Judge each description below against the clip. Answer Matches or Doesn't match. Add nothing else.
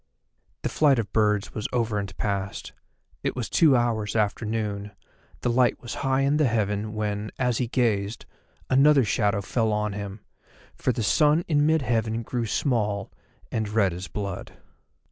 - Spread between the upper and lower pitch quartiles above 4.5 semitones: Doesn't match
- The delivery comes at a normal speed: Matches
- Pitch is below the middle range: Matches